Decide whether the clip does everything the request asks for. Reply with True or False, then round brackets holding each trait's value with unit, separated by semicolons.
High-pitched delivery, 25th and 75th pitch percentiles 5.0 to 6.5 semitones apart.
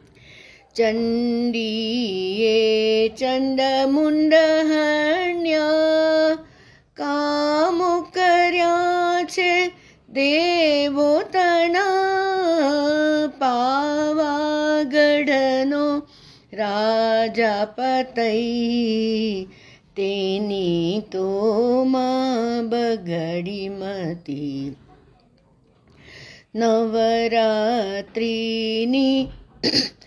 True (255 Hz; 5.6 semitones)